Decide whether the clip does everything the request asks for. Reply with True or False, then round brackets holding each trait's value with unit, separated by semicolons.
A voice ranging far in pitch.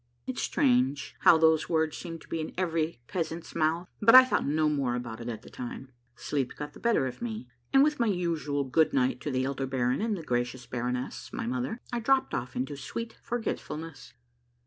True (5.7 semitones)